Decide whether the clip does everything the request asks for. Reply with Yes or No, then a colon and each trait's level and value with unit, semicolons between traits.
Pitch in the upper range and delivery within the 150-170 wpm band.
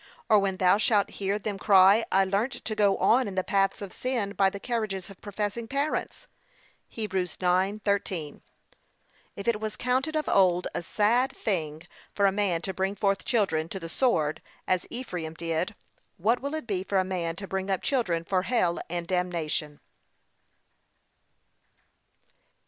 Yes: high, 195 Hz; average, 165 wpm